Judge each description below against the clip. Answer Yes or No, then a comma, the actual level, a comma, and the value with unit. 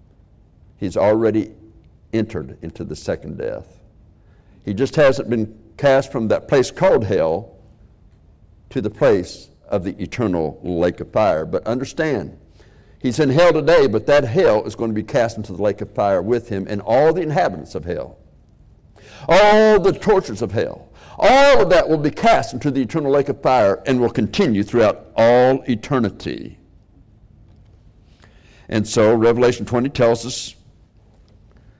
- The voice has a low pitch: Yes, low, 110 Hz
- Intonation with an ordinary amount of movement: Yes, average, 3.9 semitones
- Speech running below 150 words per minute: No, average, 155 wpm